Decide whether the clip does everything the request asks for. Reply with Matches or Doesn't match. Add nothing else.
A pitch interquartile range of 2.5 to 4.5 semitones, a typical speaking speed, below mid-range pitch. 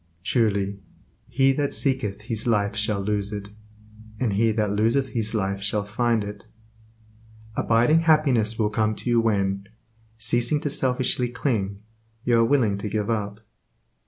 Matches